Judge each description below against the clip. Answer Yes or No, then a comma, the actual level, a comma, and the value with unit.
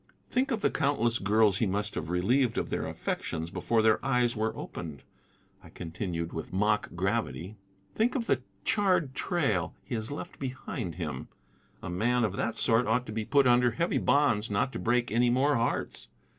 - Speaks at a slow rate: No, average, 185 wpm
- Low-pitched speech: Yes, low, 115 Hz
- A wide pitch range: No, average, 4.7 semitones